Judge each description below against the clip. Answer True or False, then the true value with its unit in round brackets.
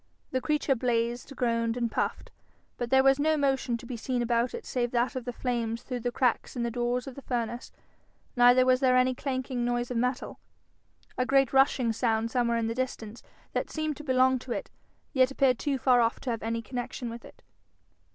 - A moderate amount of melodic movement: False (1.7 semitones)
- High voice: True (245 Hz)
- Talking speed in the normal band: False (210 wpm)